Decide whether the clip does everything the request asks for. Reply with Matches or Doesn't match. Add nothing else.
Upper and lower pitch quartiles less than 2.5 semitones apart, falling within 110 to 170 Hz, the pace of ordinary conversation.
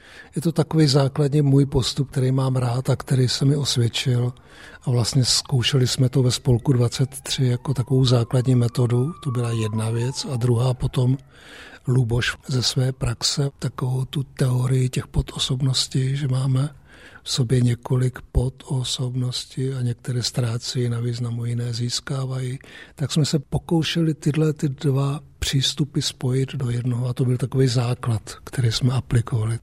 Matches